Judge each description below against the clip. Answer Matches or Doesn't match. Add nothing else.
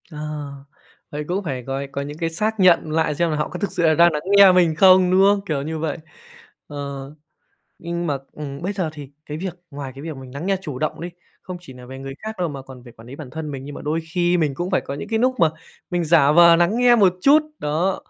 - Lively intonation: Doesn't match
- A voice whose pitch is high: Doesn't match